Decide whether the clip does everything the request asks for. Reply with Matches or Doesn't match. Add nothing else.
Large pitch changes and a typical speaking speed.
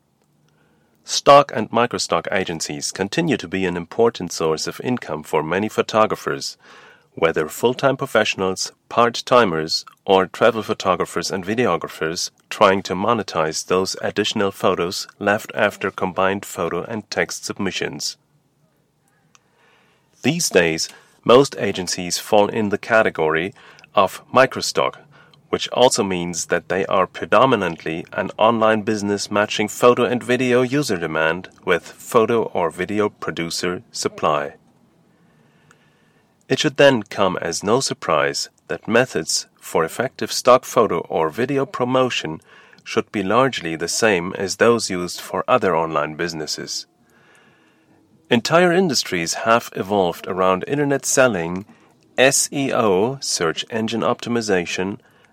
Doesn't match